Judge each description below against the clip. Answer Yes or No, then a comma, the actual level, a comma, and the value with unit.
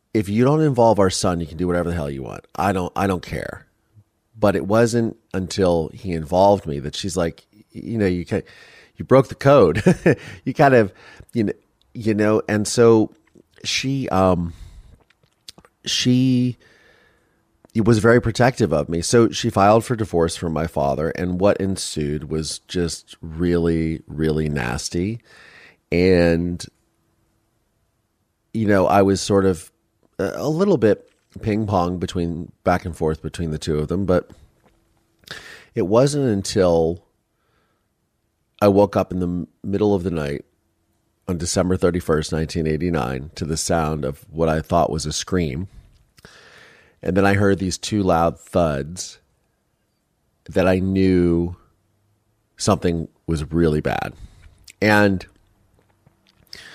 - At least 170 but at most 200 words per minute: No, average, 145 wpm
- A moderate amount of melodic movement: Yes, average, 4.3 semitones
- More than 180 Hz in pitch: No, very low, 95 Hz